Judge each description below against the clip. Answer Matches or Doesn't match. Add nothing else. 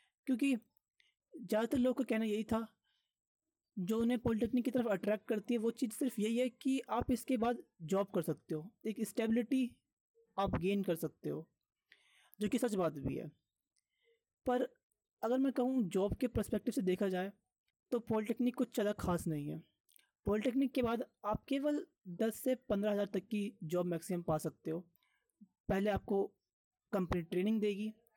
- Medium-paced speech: Matches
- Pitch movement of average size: Matches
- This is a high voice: Matches